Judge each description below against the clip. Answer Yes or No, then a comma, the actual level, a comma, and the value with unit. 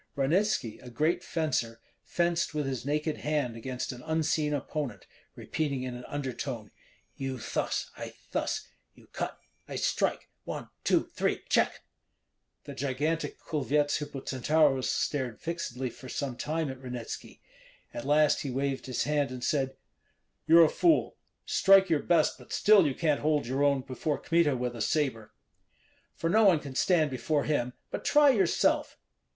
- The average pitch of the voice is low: No, medium, 145 Hz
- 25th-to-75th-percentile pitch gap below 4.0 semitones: Yes, average, 3.6 semitones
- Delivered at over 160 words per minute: No, average, 155 wpm